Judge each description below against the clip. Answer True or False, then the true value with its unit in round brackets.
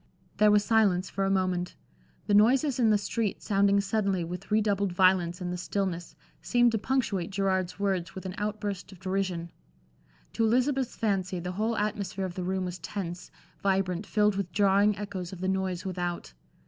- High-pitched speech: True (195 Hz)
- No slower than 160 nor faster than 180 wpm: True (175 wpm)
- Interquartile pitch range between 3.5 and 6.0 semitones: False (2.4 semitones)